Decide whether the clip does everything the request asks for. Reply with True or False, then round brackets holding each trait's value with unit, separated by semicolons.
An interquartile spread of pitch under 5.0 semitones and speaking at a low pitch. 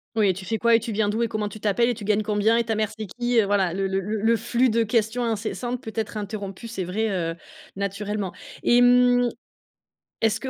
False (2.4 semitones; 220 Hz)